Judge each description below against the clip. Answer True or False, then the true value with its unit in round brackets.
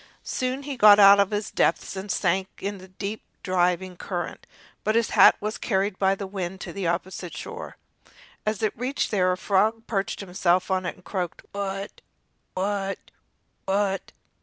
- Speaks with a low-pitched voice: False (195 Hz)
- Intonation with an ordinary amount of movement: False (1.8 semitones)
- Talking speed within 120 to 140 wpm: False (170 wpm)